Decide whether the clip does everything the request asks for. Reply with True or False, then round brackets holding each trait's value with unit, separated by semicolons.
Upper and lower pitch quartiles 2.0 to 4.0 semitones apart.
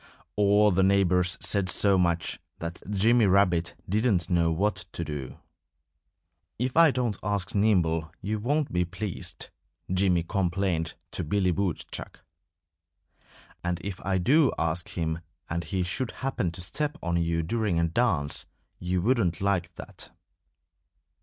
True (3.4 semitones)